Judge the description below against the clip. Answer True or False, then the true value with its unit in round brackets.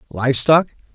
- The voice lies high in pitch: False (135 Hz)